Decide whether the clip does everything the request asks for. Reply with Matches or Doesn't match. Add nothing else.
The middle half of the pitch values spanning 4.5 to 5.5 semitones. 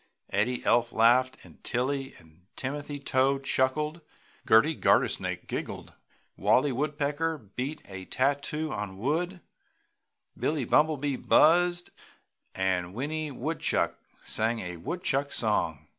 Matches